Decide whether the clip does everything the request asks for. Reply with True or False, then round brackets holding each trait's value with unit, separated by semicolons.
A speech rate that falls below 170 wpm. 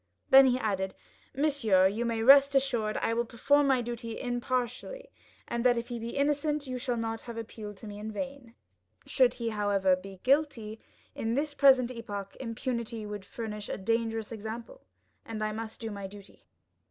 False (175 wpm)